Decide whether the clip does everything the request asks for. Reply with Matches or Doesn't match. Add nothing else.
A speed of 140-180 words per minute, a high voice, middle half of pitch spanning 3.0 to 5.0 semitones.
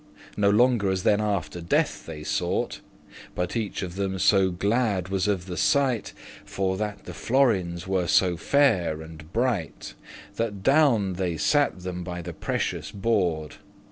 Doesn't match